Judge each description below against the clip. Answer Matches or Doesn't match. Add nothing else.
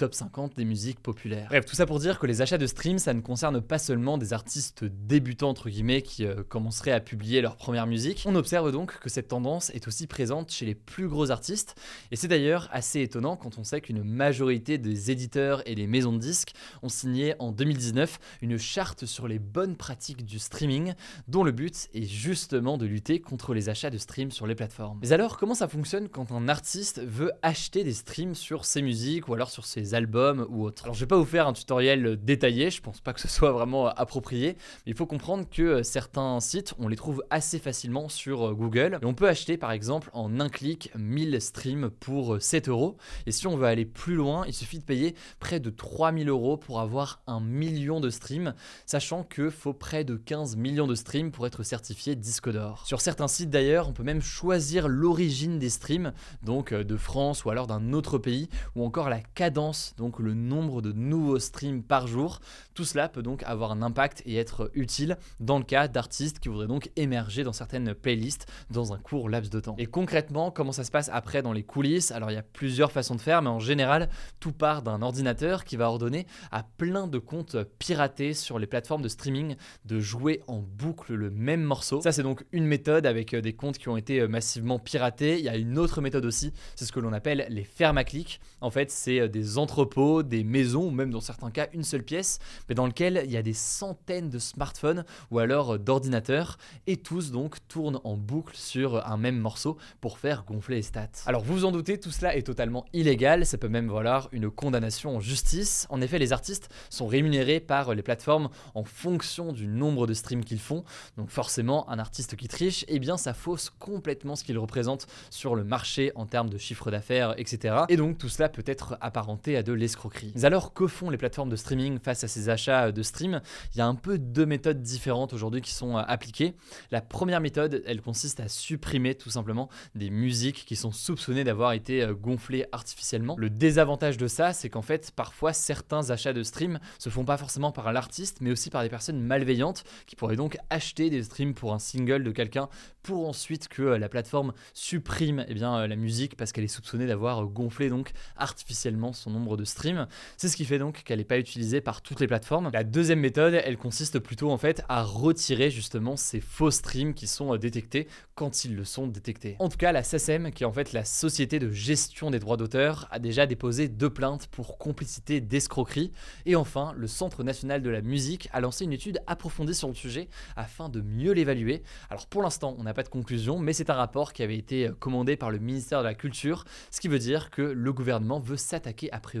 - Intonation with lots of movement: Doesn't match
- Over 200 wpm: Matches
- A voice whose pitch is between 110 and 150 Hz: Matches